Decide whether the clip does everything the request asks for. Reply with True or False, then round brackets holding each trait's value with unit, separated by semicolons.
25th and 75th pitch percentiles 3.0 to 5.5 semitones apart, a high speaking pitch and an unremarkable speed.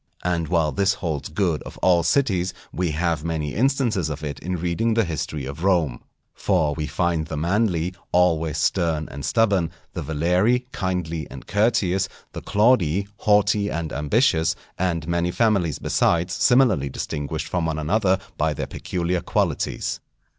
False (3.8 semitones; 85 Hz; 155 wpm)